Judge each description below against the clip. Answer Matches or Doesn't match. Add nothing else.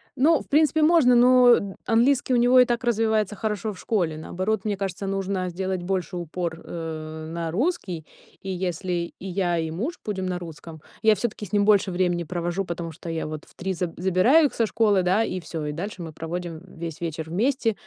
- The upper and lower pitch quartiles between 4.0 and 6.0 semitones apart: Matches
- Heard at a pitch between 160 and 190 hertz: Matches